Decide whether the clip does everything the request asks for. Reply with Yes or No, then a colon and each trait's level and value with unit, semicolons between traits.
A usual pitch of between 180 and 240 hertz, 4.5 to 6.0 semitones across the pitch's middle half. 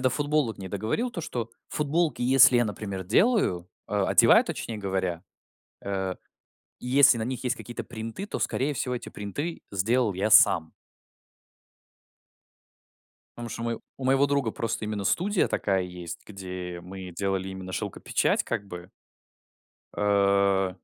No: low, 110 Hz; average, 5.2 semitones